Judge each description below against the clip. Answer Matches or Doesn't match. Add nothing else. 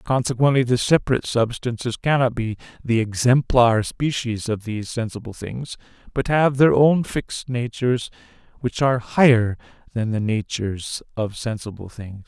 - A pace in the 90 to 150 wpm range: Matches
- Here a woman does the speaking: Doesn't match